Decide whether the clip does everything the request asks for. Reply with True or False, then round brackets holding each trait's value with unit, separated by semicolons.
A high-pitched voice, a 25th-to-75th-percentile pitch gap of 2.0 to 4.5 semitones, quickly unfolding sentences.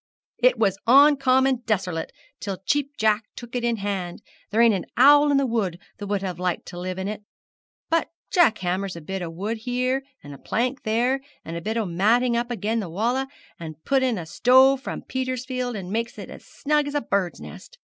False (230 Hz; 5.3 semitones; 210 wpm)